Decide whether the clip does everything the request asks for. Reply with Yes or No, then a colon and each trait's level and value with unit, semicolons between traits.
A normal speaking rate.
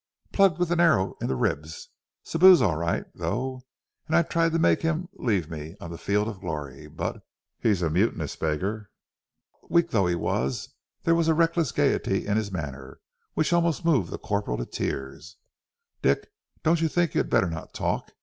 Yes: average, 190 wpm